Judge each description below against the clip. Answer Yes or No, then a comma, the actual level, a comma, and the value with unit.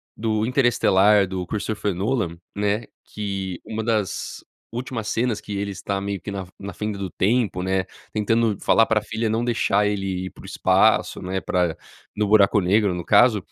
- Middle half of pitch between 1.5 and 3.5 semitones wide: Yes, narrow, 2.5 semitones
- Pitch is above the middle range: No, low, 105 Hz